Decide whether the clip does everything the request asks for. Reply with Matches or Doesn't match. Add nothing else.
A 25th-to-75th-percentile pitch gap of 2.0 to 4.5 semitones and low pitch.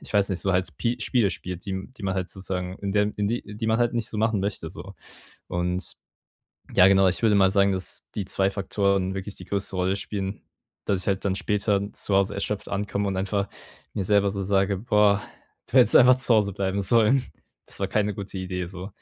Doesn't match